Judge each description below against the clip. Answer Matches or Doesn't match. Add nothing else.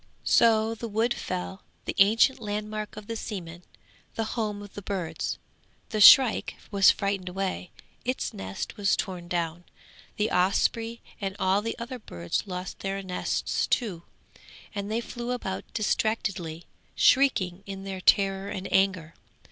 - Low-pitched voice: Doesn't match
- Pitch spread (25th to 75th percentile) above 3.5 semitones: Doesn't match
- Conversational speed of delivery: Matches